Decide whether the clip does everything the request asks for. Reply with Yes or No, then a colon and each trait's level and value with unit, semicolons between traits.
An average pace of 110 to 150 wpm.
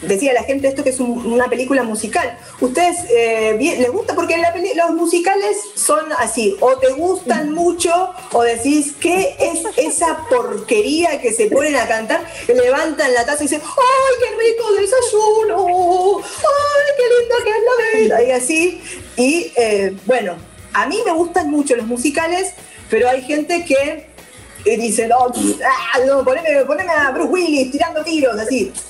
No: average, 170 wpm